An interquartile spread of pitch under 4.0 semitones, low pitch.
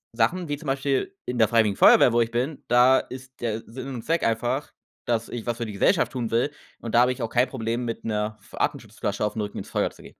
Yes: average, 2.7 semitones; low, 120 Hz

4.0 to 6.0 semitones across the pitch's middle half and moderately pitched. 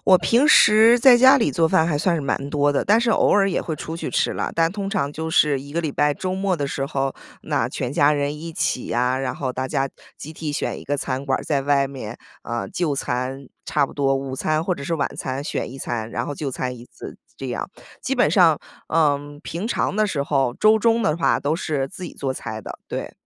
Yes: average, 4.7 semitones; medium, 145 Hz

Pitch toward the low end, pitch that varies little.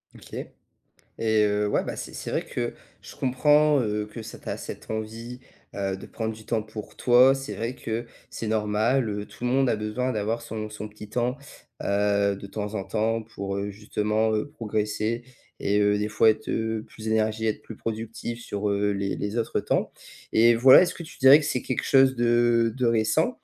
Yes: low, 110 Hz; narrow, 2.1 semitones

